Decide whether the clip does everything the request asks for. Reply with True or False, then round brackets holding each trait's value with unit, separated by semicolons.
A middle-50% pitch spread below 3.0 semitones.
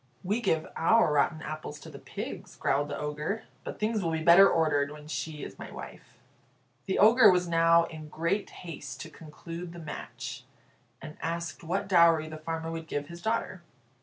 True (2.5 semitones)